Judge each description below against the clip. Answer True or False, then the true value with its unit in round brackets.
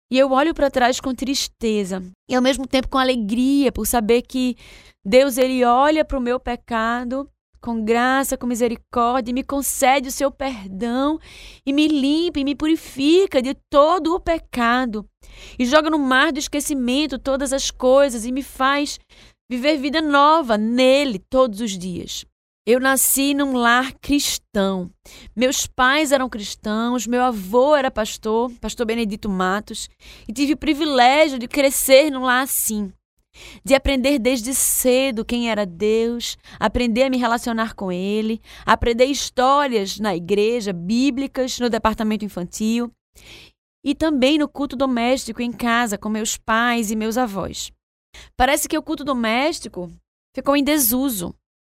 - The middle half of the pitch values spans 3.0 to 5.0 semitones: True (3.4 semitones)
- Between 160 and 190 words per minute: False (150 wpm)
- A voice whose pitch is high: True (255 Hz)